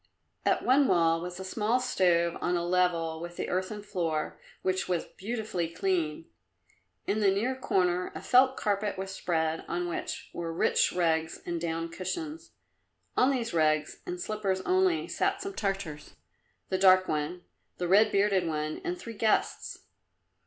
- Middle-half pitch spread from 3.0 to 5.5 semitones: Yes, average, 4.0 semitones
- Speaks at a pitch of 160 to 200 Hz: Yes, medium, 185 Hz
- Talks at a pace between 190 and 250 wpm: No, average, 160 wpm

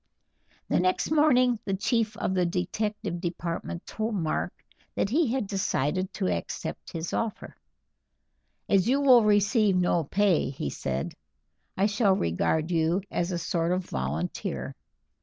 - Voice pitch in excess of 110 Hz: Yes, medium, 185 Hz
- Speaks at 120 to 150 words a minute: Yes, average, 140 wpm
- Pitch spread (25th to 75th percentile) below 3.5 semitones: No, average, 4.1 semitones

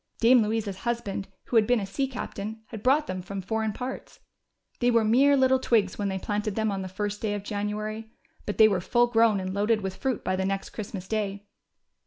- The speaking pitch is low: No, high, 215 Hz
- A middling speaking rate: No, fast, 220 wpm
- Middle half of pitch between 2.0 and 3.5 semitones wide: Yes, average, 2.7 semitones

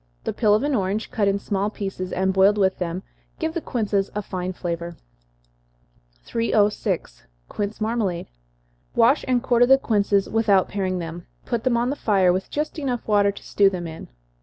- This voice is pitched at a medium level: No, high, 205 Hz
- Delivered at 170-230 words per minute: Yes, average, 180 wpm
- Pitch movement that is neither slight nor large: Yes, average, 3.7 semitones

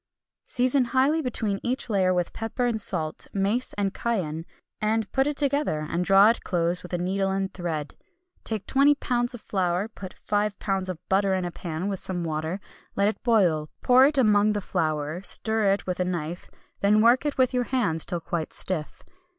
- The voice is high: Yes, high, 195 Hz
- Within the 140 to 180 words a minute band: No, average, 195 wpm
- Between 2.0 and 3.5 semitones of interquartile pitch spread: No, average, 4.9 semitones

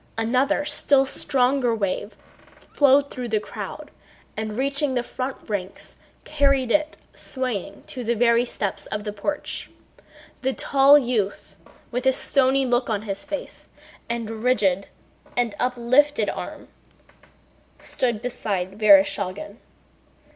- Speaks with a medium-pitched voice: No, high, 245 Hz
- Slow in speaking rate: Yes, slow, 120 wpm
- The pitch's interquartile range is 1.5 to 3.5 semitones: No, average, 4.2 semitones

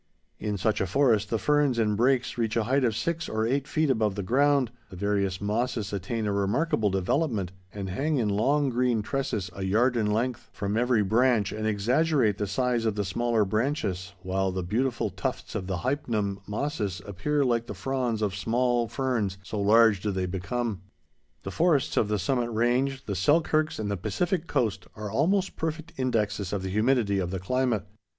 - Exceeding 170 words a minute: Yes, average, 190 wpm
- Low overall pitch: Yes, low, 110 Hz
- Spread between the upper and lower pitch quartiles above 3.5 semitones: Yes, average, 4.4 semitones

